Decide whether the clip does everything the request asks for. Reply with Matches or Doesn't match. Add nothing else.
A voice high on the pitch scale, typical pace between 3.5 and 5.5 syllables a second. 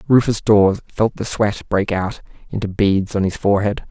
Doesn't match